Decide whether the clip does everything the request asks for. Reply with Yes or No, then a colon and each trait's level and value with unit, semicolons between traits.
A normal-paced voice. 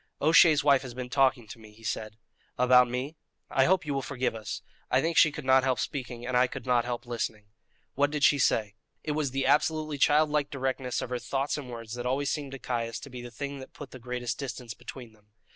No: fast, 235 wpm